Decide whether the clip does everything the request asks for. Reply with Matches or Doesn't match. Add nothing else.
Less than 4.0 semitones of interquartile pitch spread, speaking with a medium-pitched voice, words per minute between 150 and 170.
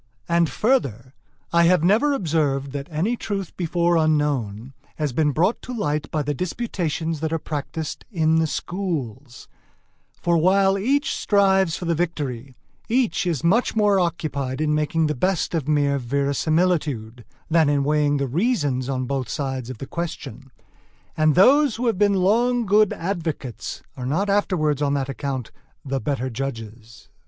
Doesn't match